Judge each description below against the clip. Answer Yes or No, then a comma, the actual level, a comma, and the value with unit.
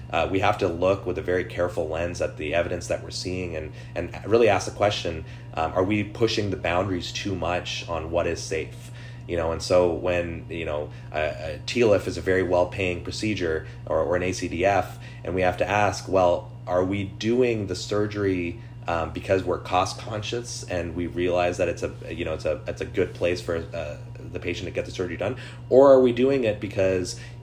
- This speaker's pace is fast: Yes, fast, 210 wpm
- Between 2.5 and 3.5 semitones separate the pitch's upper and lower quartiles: No, average, 5.1 semitones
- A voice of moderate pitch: No, very low, 95 Hz